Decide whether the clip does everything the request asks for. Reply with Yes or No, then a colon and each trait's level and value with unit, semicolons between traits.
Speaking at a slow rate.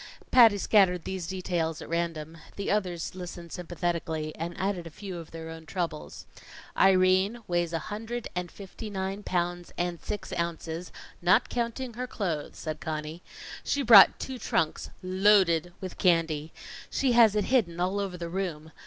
No: average, 160 wpm